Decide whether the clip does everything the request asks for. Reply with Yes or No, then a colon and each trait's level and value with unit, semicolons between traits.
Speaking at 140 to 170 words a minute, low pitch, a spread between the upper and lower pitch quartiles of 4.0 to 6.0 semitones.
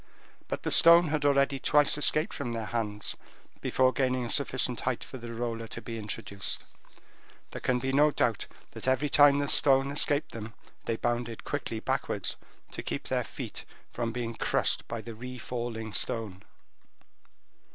No: average, 160 wpm; low, 125 Hz; average, 3.5 semitones